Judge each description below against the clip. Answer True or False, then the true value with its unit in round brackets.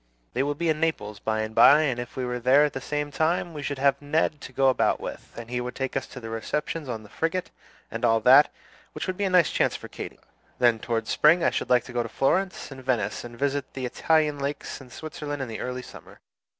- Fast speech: True (255 wpm)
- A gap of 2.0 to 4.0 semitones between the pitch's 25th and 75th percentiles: True (3.6 semitones)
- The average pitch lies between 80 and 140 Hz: True (135 Hz)